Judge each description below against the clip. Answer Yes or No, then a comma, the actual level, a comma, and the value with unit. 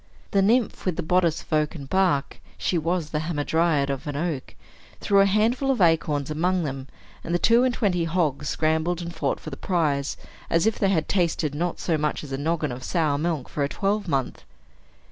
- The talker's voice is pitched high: No, medium, 165 Hz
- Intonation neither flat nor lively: Yes, average, 3.6 semitones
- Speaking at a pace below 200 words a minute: No, fast, 205 wpm